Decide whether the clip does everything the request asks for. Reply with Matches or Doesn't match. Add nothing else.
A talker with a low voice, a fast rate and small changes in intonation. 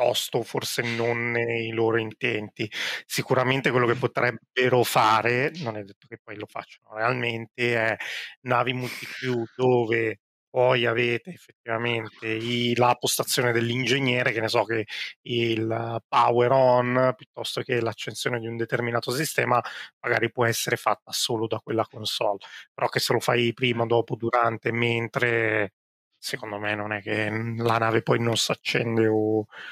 Doesn't match